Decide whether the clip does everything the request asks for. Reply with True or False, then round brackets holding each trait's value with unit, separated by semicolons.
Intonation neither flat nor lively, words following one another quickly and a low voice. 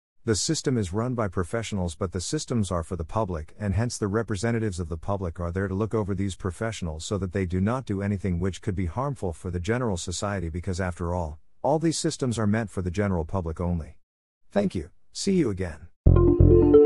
True (4.0 semitones; 215 wpm; 100 Hz)